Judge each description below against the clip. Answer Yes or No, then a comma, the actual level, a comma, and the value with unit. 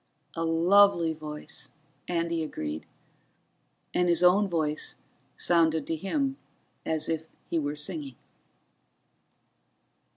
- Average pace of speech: No, slow, 100 wpm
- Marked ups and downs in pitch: No, narrow, 2.5 semitones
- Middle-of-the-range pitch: Yes, medium, 165 Hz